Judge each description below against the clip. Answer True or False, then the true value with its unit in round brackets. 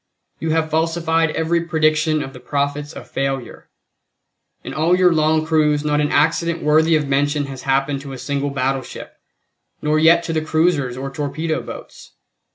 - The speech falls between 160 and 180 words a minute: True (165 wpm)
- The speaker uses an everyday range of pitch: False (2.3 semitones)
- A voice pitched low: False (155 Hz)